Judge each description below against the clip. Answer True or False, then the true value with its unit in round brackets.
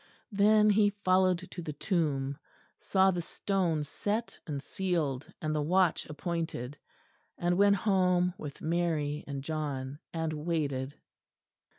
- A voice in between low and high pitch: True (165 Hz)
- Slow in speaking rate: True (125 wpm)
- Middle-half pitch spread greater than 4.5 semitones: False (4.2 semitones)